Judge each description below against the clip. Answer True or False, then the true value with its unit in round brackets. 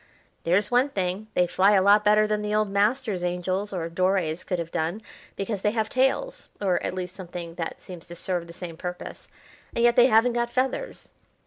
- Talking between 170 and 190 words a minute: False (205 wpm)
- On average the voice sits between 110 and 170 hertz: False (195 Hz)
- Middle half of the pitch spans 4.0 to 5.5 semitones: False (3.5 semitones)